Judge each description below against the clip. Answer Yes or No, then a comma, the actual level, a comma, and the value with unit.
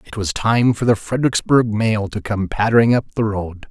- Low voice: Yes, low, 110 Hz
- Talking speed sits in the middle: No, fast, 210 wpm